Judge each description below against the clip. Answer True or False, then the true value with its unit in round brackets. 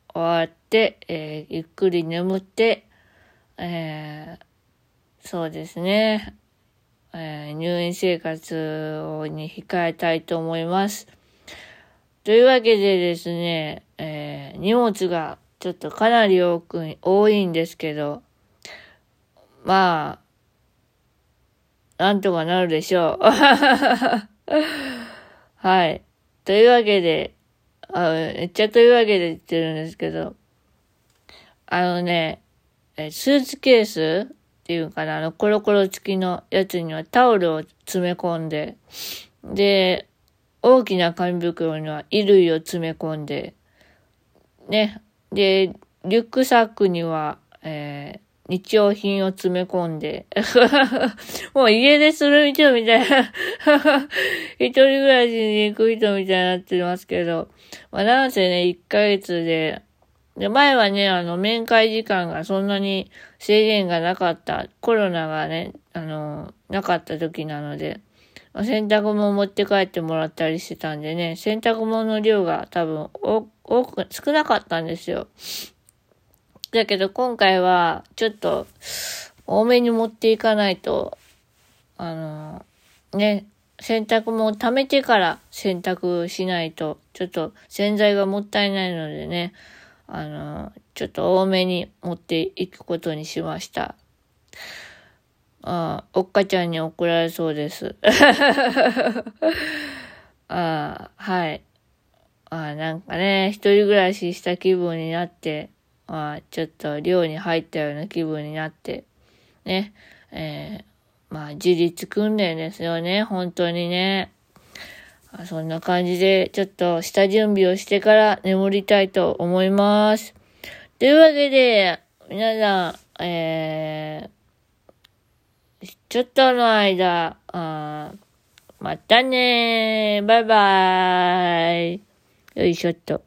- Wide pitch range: False (4.5 semitones)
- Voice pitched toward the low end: False (185 Hz)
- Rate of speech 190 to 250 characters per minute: True (225 characters per minute)